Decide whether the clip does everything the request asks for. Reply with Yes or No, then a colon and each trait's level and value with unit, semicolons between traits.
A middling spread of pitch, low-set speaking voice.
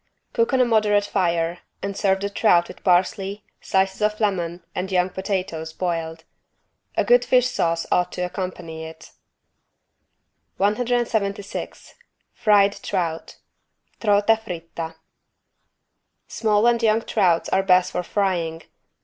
No: average, 3.4 semitones; high, 190 Hz